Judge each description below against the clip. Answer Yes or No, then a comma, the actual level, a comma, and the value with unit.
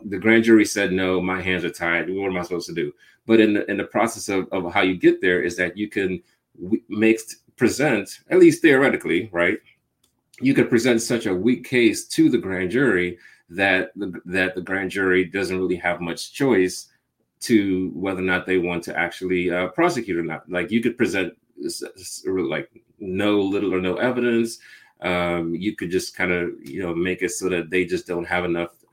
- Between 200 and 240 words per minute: Yes, fast, 205 wpm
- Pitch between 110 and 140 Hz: No, very low, 95 Hz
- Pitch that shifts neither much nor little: Yes, average, 3.6 semitones